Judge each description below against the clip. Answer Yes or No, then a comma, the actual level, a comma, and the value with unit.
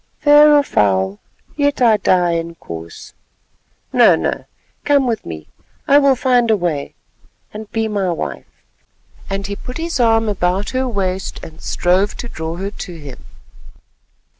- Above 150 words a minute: No, average, 140 wpm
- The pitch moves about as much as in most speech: No, wide, 6.6 semitones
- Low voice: No, high, 200 Hz